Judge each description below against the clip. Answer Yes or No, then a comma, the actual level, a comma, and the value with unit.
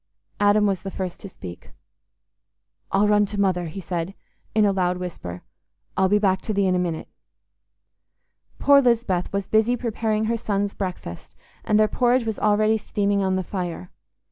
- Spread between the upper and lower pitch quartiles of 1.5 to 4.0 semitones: Yes, average, 2.8 semitones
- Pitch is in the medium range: No, high, 200 Hz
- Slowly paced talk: No, average, 170 wpm